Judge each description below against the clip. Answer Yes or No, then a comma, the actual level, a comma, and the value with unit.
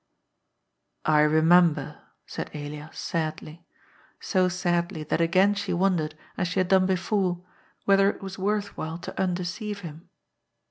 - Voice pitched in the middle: Yes, medium, 180 Hz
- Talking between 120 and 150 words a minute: Yes, average, 140 wpm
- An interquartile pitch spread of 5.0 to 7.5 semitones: No, average, 3.2 semitones